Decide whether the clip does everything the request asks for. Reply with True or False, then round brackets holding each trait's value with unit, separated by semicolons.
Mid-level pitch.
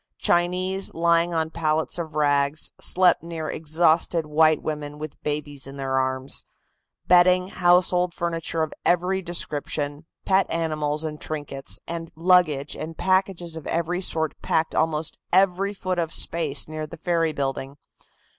True (160 Hz)